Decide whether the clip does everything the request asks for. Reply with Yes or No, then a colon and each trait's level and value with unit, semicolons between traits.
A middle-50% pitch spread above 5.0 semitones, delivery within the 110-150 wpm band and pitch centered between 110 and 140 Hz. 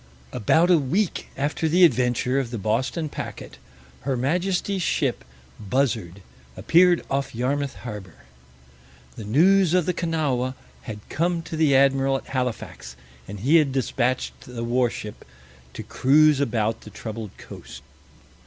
Yes: wide, 5.4 semitones; slow, 135 wpm; low, 135 Hz